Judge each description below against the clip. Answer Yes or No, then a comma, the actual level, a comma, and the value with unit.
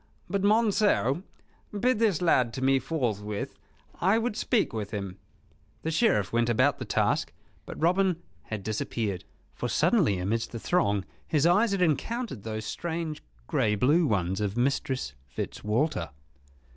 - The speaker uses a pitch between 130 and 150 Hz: Yes, low, 135 Hz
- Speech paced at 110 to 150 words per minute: Yes, average, 145 wpm